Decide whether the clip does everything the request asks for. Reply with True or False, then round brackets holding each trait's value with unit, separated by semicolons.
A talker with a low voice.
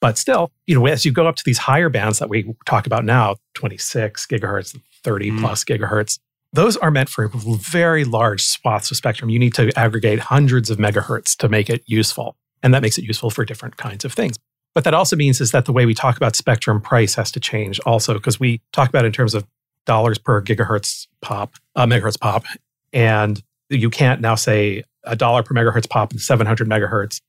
True (120 Hz)